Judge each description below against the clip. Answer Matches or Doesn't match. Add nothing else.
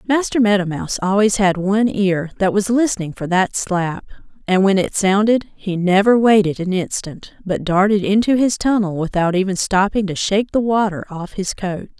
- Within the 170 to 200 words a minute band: Matches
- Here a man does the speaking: Doesn't match